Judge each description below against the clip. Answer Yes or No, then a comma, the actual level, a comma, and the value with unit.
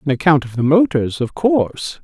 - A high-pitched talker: No, medium, 145 Hz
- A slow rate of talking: No, fast, 205 wpm